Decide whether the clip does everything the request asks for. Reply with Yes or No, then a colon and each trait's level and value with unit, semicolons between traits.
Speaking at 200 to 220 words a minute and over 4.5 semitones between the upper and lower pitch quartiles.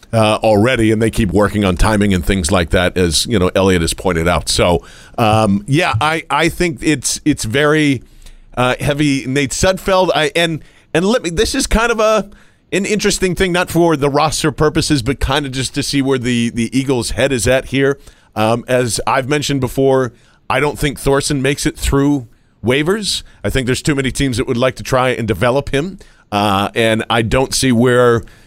Yes: fast, 205 wpm; average, 5.2 semitones